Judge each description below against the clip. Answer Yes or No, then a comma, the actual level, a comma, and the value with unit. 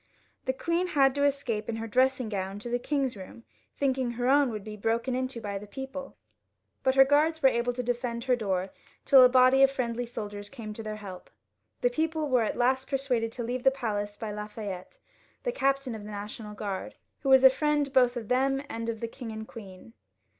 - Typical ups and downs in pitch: Yes, average, 3.8 semitones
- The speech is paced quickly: Yes, fast, 215 wpm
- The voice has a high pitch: Yes, high, 245 Hz